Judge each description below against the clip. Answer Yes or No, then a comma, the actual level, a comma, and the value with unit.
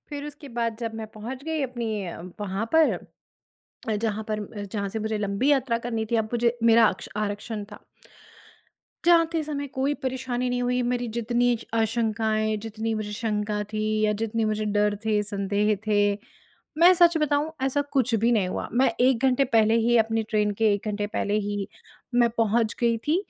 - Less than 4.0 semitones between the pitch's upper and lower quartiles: Yes, average, 2.9 semitones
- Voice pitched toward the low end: No, high, 225 Hz